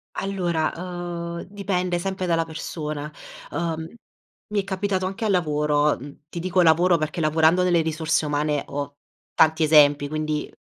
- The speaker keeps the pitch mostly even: No, average, 3.0 semitones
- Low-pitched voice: No, medium, 165 Hz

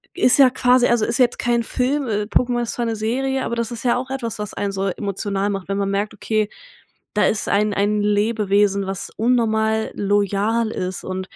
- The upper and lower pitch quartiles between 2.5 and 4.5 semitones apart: Yes, average, 2.9 semitones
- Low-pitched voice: No, high, 215 Hz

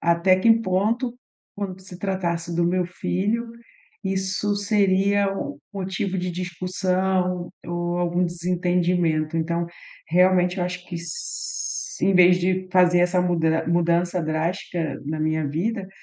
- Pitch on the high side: No, medium, 180 Hz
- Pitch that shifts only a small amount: Yes, narrow, 1.8 semitones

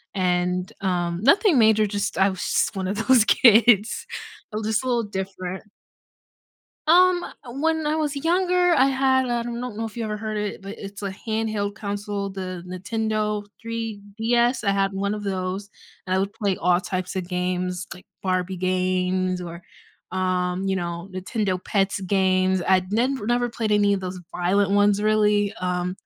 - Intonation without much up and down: No, average, 3.3 semitones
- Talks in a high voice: Yes, high, 200 Hz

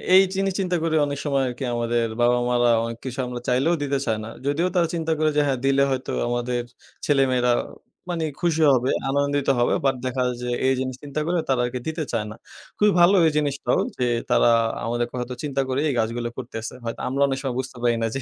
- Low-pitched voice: Yes, low, 130 Hz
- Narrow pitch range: No, average, 3.0 semitones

